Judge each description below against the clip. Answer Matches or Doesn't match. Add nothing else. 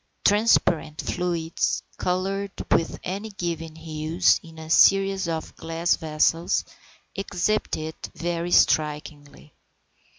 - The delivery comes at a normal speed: Doesn't match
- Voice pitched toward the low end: Doesn't match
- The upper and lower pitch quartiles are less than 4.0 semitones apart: Matches